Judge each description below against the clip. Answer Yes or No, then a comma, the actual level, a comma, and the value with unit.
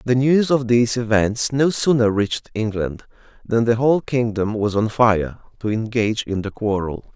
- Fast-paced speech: No, average, 175 wpm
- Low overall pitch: Yes, low, 115 Hz